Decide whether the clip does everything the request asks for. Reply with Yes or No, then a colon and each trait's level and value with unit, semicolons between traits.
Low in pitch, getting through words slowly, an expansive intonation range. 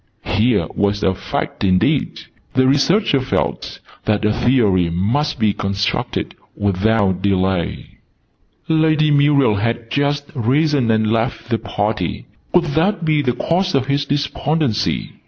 Yes: low, 120 Hz; slow, 130 wpm; wide, 6.0 semitones